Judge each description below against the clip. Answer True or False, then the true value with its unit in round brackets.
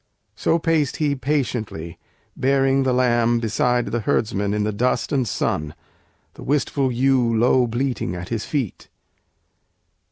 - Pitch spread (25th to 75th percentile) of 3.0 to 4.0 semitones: True (3.5 semitones)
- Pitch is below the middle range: True (125 Hz)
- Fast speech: False (135 wpm)